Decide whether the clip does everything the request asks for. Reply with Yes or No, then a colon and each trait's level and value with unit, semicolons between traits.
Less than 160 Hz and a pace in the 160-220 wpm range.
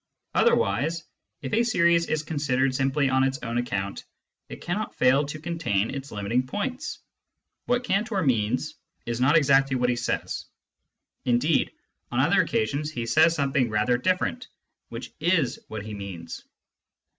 No: low, 135 Hz; average, 145 wpm